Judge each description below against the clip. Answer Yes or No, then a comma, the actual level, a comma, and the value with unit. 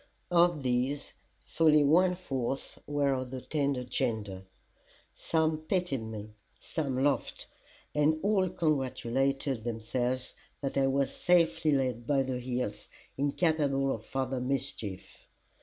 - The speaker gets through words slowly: Yes, slow, 120 wpm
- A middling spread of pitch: Yes, average, 3.4 semitones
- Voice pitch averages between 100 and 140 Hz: Yes, low, 135 Hz